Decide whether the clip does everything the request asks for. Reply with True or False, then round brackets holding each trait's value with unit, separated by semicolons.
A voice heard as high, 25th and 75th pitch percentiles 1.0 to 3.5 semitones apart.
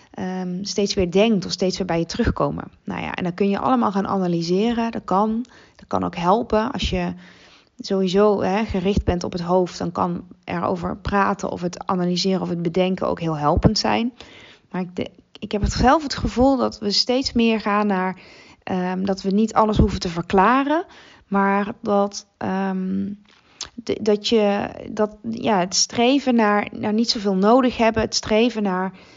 True (200 Hz; 3.2 semitones)